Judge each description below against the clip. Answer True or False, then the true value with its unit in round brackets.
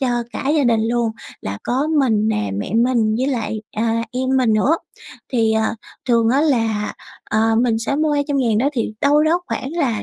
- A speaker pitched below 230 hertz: False (235 Hz)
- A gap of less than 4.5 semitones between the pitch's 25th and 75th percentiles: True (3.9 semitones)